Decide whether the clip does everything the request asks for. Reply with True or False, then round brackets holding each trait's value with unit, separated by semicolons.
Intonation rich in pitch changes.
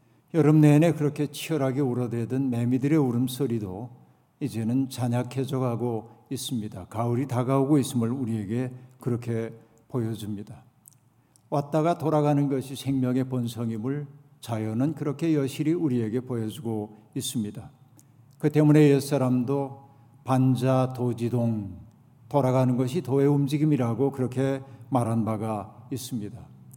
False (2.9 semitones)